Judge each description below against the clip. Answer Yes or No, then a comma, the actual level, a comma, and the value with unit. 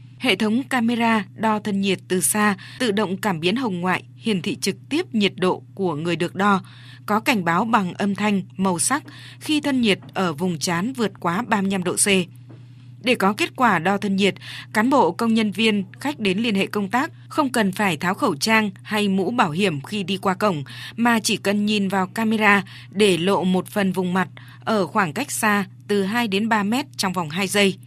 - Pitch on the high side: Yes, high, 200 Hz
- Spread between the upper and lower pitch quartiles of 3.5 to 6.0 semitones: No, average, 3.1 semitones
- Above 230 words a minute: No, average, 215 wpm